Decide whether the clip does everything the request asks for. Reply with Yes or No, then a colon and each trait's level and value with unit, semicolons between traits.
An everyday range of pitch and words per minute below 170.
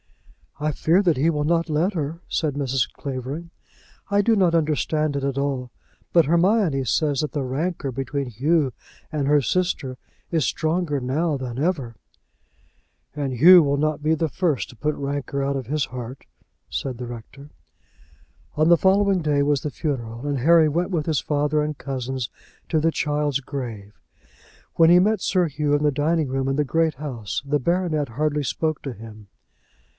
No: average, 3.2 semitones; average, 175 wpm